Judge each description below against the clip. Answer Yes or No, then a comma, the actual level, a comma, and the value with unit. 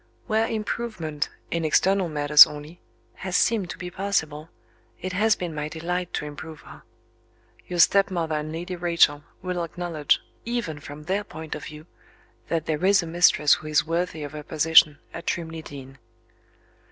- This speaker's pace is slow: No, average, 165 wpm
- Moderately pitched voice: Yes, medium, 165 Hz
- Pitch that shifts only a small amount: No, average, 3.2 semitones